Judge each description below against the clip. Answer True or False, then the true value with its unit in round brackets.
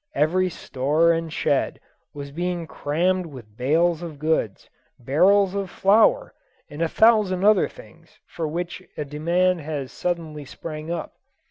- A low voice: False (165 Hz)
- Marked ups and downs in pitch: False (3.6 semitones)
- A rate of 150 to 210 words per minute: False (140 wpm)